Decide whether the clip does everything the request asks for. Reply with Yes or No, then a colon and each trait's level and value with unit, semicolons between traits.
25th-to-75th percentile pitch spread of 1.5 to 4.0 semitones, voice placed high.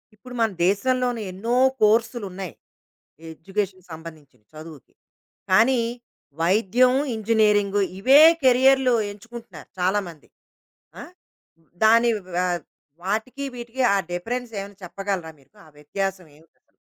No: average, 4.8 semitones; high, 205 Hz